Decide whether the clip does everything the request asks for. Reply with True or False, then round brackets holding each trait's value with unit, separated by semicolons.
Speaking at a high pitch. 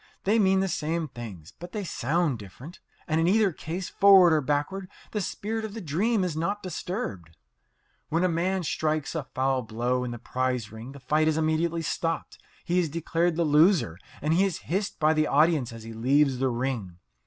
False (155 Hz)